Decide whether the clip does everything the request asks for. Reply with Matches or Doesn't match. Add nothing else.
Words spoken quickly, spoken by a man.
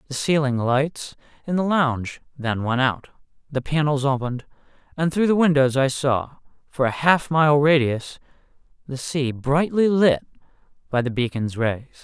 Doesn't match